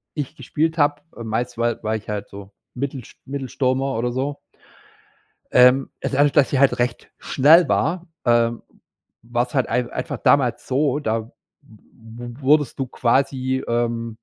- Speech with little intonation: No, average, 3.1 semitones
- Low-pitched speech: Yes, low, 130 Hz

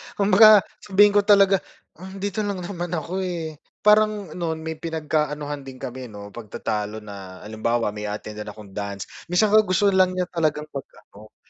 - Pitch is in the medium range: Yes, medium, 160 Hz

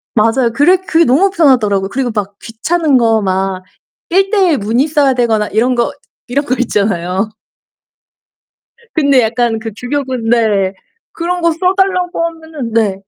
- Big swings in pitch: Yes, wide, 6.7 semitones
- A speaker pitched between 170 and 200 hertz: No, high, 245 Hz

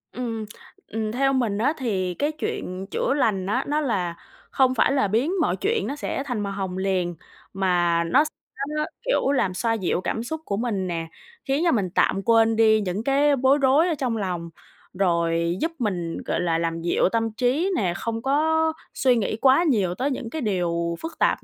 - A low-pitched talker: No, high, 225 Hz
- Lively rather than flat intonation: Yes, wide, 6.8 semitones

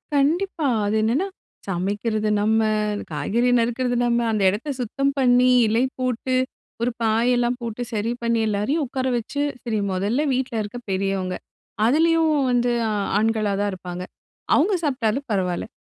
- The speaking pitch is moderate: No, high, 235 Hz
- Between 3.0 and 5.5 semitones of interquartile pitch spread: Yes, average, 3.6 semitones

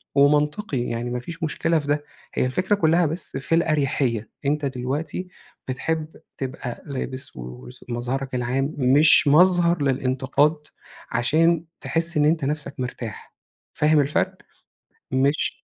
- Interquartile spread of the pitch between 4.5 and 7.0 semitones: No, average, 3.6 semitones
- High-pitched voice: No, medium, 140 Hz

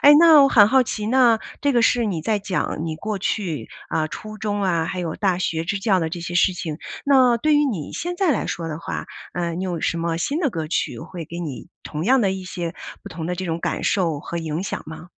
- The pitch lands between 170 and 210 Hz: Yes, medium, 185 Hz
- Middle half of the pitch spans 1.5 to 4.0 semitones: No, average, 5.3 semitones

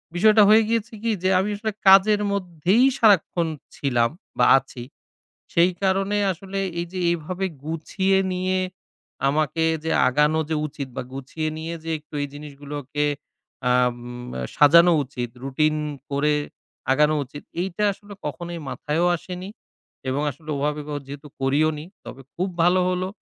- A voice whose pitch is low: No, medium, 160 Hz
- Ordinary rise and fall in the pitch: Yes, average, 4.5 semitones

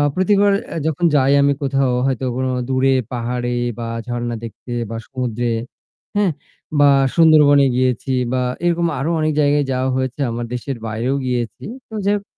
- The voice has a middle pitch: No, low, 130 Hz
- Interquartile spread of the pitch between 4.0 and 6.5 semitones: No, average, 3.3 semitones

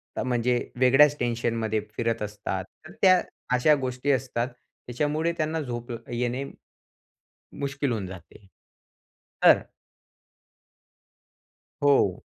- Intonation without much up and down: No, average, 3.5 semitones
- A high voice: No, low, 125 Hz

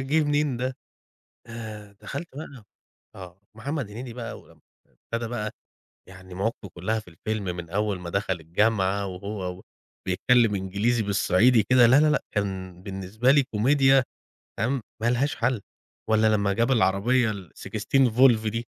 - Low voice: Yes, low, 110 Hz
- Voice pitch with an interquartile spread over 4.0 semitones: Yes, average, 4.4 semitones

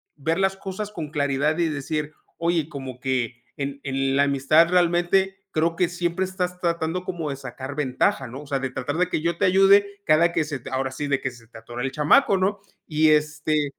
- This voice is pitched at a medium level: Yes, medium, 155 Hz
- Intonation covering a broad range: No, average, 4.3 semitones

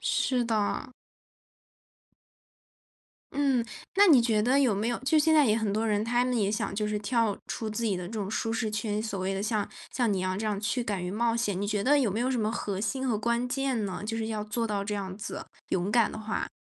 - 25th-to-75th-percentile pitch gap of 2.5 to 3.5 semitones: Yes, average, 2.8 semitones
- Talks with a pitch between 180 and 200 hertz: No, high, 220 Hz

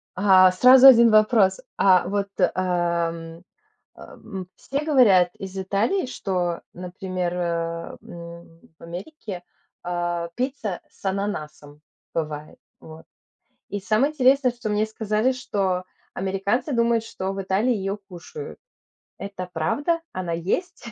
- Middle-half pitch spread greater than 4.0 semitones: Yes, average, 4.8 semitones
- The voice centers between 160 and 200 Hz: Yes, high, 190 Hz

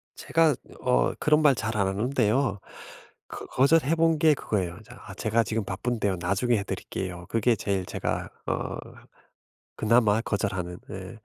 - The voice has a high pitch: No, low, 110 Hz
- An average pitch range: Yes, average, 4.9 semitones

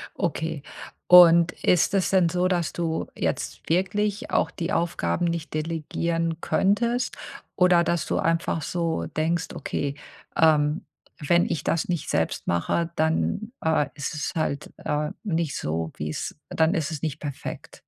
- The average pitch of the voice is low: No, medium, 165 Hz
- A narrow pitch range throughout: Yes, narrow, 2.3 semitones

